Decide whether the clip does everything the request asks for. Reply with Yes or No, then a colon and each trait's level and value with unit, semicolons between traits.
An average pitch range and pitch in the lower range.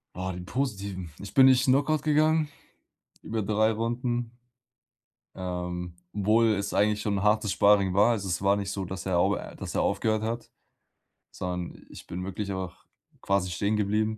Yes: average, 3.2 semitones; low, 105 Hz